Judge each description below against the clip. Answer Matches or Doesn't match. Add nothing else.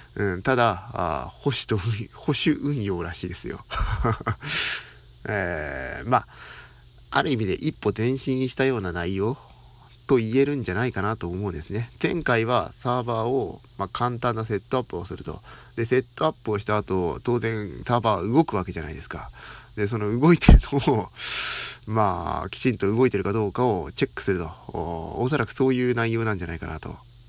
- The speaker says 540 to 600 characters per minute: Doesn't match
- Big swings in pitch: Doesn't match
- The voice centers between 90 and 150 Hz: Matches